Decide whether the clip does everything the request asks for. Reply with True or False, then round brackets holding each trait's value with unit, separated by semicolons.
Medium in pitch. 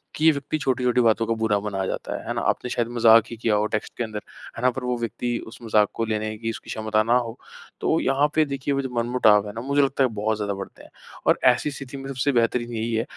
False (115 Hz)